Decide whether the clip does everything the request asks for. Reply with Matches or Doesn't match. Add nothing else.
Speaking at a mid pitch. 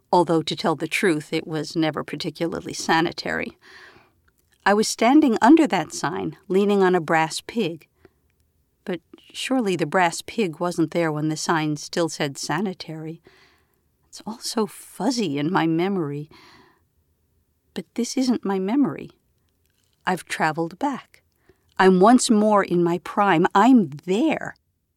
Matches